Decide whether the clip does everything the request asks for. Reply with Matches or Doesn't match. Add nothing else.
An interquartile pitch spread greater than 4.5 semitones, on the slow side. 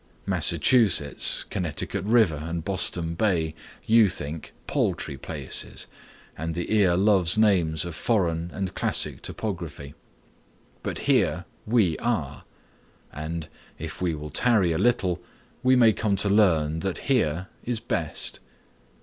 Matches